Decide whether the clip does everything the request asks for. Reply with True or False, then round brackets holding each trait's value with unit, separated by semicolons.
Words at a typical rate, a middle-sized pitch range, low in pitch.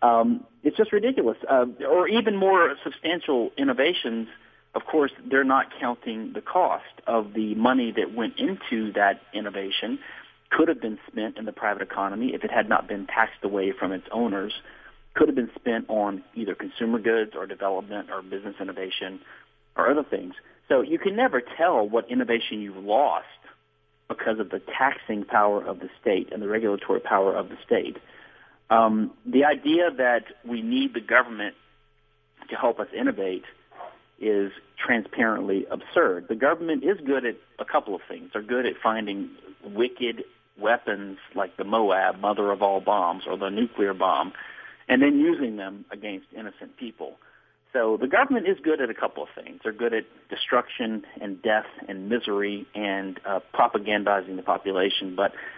False (165 wpm; 7.5 semitones; 115 Hz)